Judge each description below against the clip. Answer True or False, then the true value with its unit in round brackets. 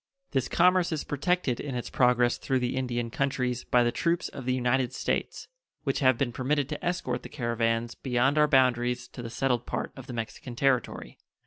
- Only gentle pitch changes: True (2.2 semitones)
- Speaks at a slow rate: False (195 wpm)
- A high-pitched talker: False (125 Hz)